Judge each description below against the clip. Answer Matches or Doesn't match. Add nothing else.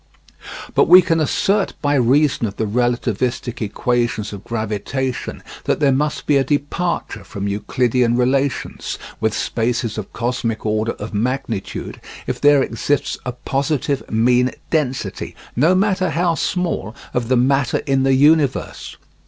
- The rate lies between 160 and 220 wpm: Doesn't match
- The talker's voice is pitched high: Doesn't match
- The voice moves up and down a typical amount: Matches